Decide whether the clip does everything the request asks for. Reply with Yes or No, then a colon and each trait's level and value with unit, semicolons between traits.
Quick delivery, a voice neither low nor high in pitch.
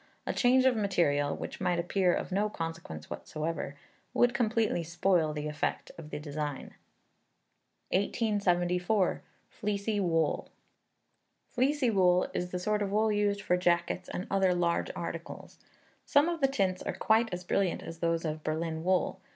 No: average, 150 wpm; medium, 180 Hz